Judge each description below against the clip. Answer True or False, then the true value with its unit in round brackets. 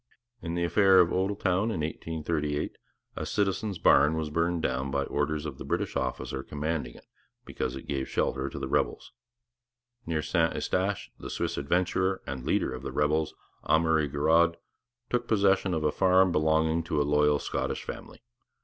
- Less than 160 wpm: False (165 wpm)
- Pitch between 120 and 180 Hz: False (80 Hz)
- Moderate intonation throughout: True (3.7 semitones)